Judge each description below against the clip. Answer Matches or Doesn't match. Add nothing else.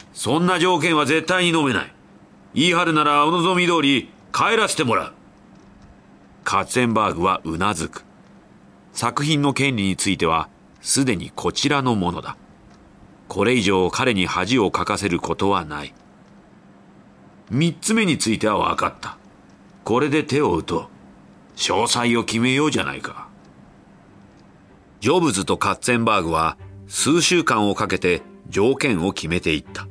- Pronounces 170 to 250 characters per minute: Doesn't match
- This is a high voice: Doesn't match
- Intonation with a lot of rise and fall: Matches